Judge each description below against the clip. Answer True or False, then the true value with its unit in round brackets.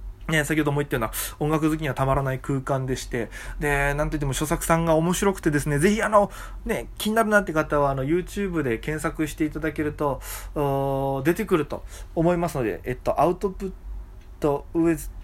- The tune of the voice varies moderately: True (3.8 semitones)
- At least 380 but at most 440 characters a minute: True (415 characters per minute)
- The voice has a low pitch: False (150 Hz)